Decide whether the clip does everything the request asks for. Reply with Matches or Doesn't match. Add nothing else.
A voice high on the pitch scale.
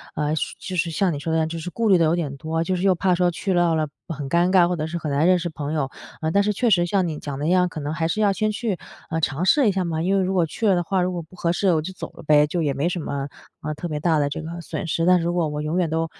Doesn't match